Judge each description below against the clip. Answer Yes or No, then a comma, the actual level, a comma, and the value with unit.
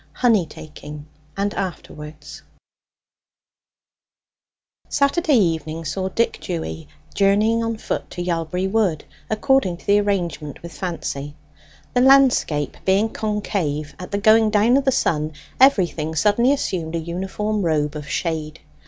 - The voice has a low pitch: No, medium, 185 Hz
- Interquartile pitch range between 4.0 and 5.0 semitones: No, wide, 5.4 semitones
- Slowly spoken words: Yes, slow, 125 wpm